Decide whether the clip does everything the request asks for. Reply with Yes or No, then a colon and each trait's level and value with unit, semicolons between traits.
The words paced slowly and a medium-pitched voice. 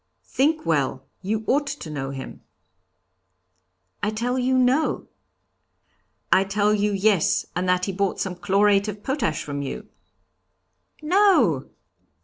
No: slow, 130 wpm; high, 205 Hz